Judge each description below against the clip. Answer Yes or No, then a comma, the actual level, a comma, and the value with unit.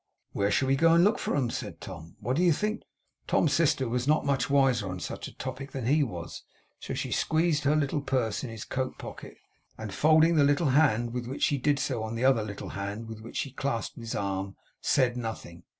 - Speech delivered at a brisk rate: Yes, fast, 230 wpm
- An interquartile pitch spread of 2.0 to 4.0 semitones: No, average, 4.5 semitones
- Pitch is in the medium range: No, low, 130 Hz